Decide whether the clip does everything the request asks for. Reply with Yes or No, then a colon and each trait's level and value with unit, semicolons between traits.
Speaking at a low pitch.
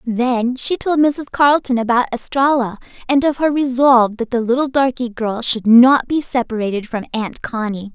No: high, 245 Hz